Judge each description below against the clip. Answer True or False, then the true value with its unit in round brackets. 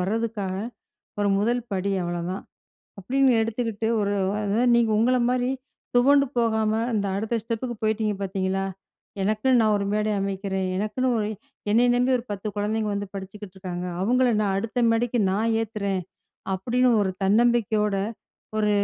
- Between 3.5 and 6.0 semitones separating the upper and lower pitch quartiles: False (3.1 semitones)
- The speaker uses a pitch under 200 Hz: False (215 Hz)